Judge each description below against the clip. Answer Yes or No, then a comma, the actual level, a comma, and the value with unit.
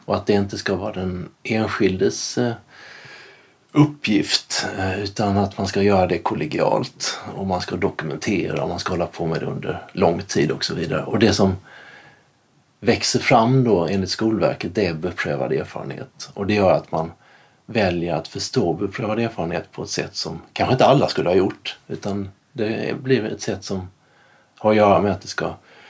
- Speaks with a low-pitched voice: Yes, low, 100 Hz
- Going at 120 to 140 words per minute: No, average, 180 wpm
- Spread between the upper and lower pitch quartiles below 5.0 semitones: Yes, average, 3.1 semitones